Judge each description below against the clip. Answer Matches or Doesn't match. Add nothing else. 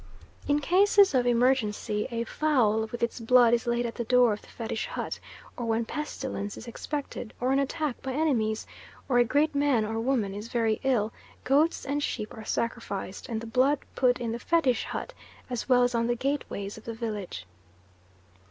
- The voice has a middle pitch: Doesn't match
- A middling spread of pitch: Matches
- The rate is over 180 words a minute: Matches